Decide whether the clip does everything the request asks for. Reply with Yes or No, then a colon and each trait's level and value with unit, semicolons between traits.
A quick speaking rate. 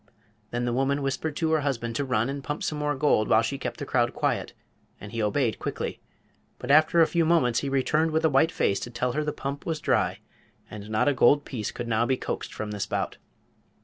Yes: fast, 235 wpm